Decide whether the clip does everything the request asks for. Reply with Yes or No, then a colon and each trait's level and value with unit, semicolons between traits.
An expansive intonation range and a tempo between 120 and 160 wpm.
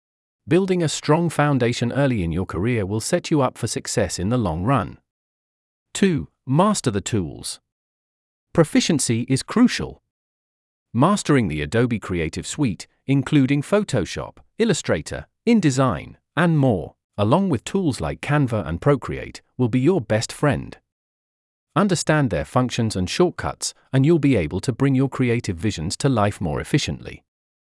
Yes: wide, 6.0 semitones; average, 145 wpm